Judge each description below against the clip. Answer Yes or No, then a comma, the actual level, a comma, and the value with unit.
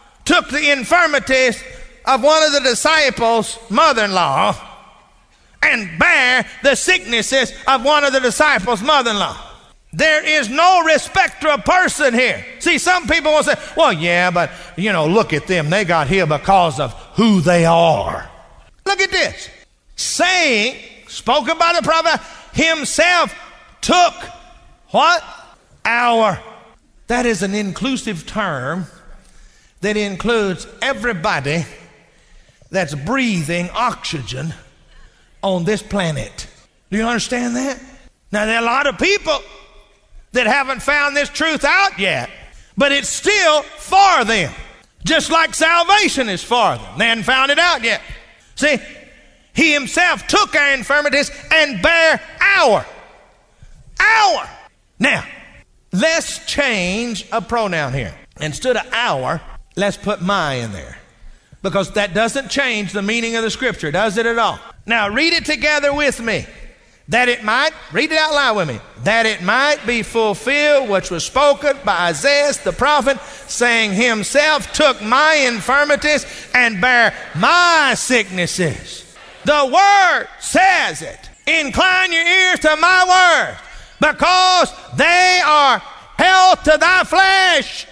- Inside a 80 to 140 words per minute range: Yes, slow, 135 wpm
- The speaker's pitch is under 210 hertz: No, very high, 265 Hz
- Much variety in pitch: Yes, wide, 6.7 semitones